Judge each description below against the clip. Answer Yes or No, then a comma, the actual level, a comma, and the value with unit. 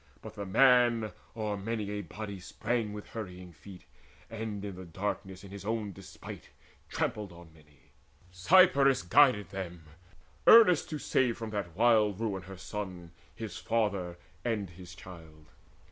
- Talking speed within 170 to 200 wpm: No, average, 145 wpm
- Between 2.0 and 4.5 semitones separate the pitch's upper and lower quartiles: Yes, average, 3.9 semitones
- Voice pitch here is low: Yes, low, 100 Hz